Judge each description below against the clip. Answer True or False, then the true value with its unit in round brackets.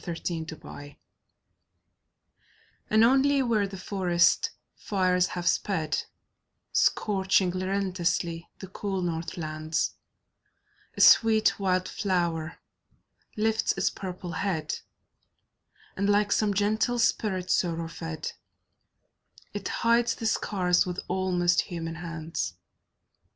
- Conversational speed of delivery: False (100 wpm)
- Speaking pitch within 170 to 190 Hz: True (185 Hz)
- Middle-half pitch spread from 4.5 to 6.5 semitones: False (3.4 semitones)